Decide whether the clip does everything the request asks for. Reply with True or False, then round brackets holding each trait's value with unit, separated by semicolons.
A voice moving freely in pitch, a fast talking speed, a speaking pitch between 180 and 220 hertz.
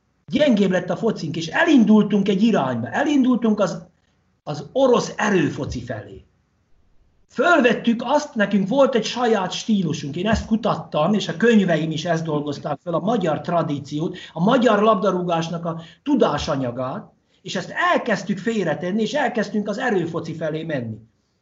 False (6.2 semitones; 135 wpm; 185 Hz)